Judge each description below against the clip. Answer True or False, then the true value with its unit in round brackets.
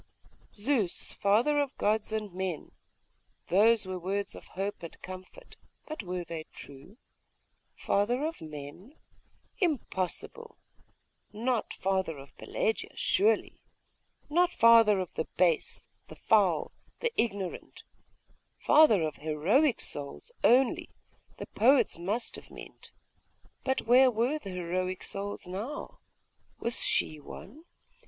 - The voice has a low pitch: False (205 Hz)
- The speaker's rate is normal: False (120 wpm)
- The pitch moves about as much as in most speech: False (6.4 semitones)